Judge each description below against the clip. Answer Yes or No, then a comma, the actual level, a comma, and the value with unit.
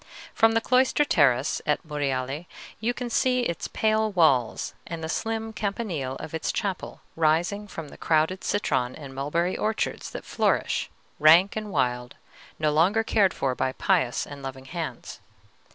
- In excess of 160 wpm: No, average, 155 wpm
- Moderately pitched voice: Yes, medium, 165 Hz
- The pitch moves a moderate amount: No, wide, 7.5 semitones